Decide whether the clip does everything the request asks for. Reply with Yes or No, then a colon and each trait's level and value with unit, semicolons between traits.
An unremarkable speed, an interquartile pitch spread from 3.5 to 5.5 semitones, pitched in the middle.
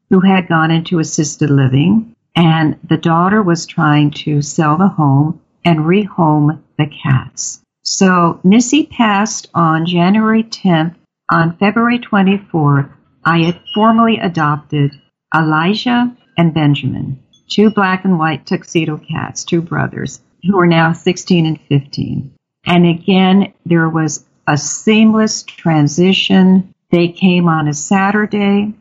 No: slow, 125 wpm; average, 4.3 semitones; medium, 170 Hz